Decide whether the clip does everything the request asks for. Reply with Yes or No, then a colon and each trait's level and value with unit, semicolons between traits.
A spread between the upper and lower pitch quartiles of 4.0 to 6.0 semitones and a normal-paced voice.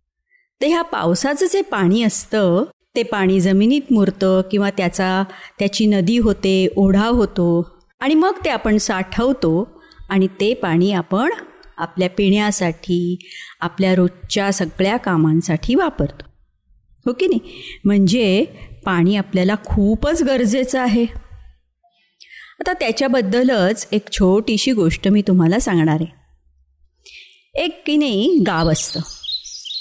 Yes: average, 5.2 semitones; average, 115 wpm